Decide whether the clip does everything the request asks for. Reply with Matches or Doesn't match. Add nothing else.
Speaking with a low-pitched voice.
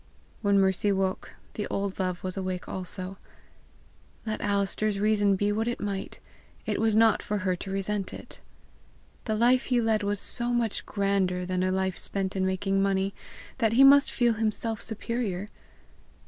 Doesn't match